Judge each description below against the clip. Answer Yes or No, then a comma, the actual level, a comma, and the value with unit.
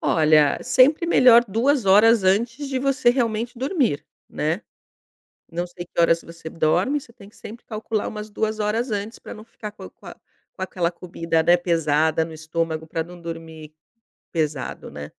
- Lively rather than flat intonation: Yes, wide, 6.0 semitones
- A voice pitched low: No, high, 190 Hz